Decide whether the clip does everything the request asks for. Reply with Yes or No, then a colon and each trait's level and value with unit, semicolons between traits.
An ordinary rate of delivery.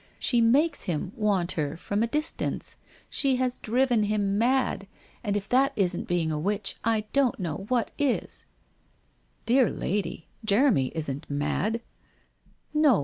Yes: average, 155 wpm